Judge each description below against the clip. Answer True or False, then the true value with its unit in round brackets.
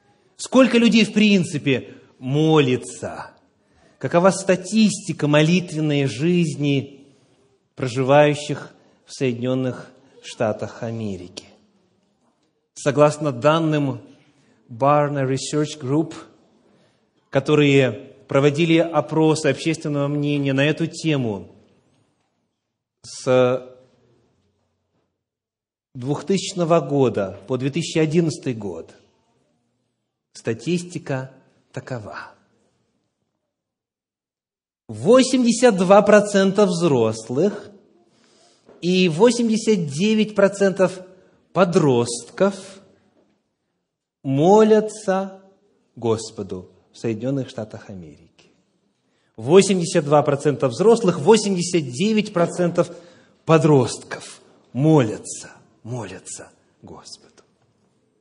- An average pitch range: False (6.3 semitones)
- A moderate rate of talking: False (55 wpm)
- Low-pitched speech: False (150 Hz)